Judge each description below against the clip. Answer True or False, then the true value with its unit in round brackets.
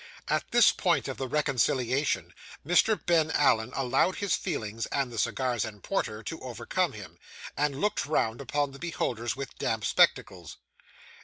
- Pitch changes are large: False (4.9 semitones)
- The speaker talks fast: False (155 wpm)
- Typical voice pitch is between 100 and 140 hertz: True (135 Hz)